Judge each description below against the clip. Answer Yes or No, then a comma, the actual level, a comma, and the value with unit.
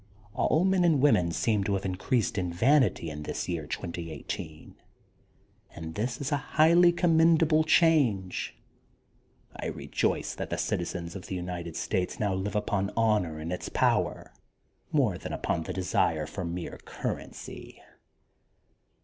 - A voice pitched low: Yes, very low, 95 Hz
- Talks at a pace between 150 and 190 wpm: No, average, 140 wpm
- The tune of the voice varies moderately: No, wide, 9.0 semitones